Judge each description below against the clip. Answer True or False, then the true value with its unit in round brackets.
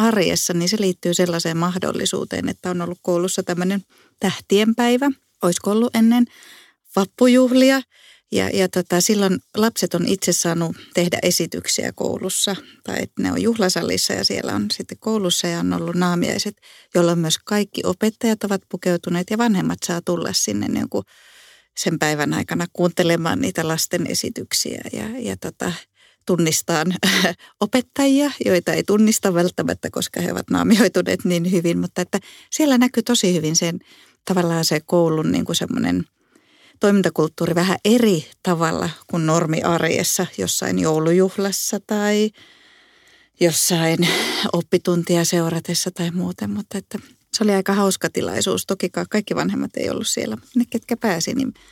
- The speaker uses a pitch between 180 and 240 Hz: True (185 Hz)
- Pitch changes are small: False (3.8 semitones)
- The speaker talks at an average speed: True (140 wpm)